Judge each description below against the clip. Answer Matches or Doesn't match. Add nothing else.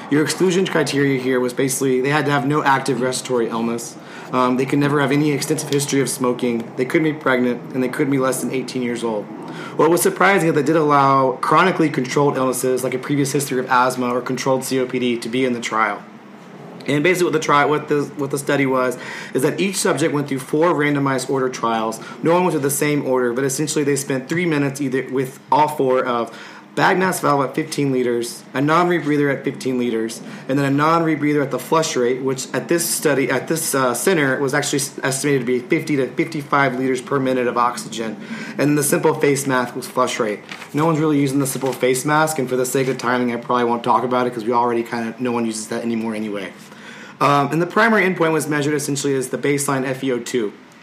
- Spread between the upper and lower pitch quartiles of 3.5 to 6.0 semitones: Doesn't match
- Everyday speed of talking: Doesn't match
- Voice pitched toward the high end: Doesn't match